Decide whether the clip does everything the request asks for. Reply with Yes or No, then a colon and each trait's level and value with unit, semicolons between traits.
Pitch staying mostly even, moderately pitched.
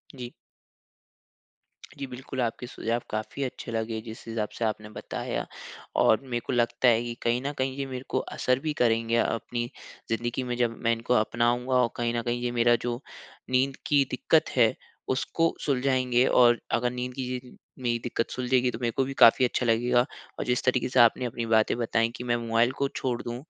No: narrow, 1.5 semitones; low, 120 Hz